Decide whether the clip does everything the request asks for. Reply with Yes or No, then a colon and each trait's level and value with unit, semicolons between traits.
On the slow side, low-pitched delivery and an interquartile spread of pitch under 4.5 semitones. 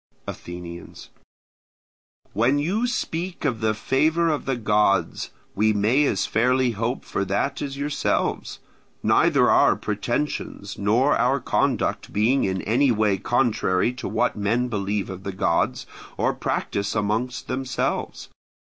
No: slow, 130 wpm; low, 115 Hz; average, 4.8 semitones